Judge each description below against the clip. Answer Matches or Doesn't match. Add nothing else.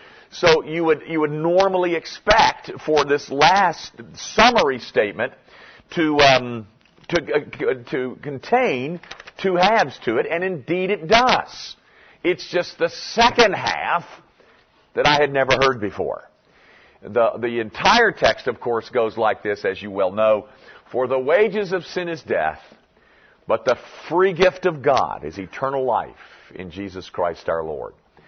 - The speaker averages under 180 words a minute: Matches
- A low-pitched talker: Doesn't match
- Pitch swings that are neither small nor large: Doesn't match